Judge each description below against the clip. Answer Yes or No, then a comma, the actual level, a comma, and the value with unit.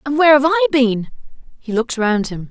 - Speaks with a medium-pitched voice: No, very high, 265 Hz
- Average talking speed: No, fast, 215 wpm